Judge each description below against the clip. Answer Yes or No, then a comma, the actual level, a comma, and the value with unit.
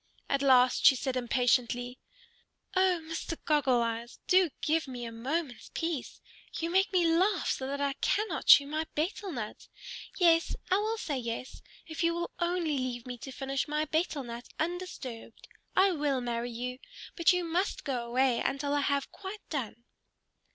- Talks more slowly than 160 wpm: No, average, 170 wpm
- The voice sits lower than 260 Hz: No, very high, 285 Hz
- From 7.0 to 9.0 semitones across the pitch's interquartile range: No, average, 5.3 semitones